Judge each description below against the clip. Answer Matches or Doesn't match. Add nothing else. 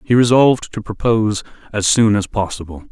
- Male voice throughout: Matches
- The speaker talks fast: Doesn't match